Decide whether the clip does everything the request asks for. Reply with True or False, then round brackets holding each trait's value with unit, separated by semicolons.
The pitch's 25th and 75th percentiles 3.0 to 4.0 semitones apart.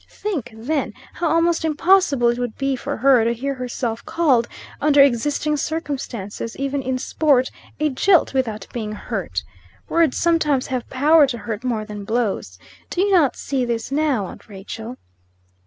False (4.7 semitones)